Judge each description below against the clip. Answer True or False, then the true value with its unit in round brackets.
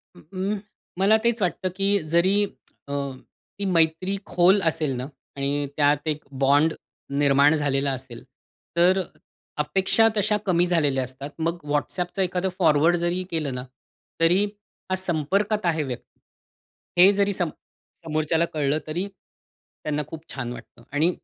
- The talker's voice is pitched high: False (165 Hz)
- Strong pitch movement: False (4.3 semitones)